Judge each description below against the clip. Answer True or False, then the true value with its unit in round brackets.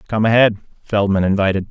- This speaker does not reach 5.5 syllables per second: False (6.1 syllables/s)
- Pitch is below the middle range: True (100 Hz)